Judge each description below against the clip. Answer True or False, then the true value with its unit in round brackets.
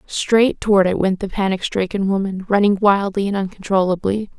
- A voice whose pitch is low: False (195 Hz)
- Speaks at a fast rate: False (165 wpm)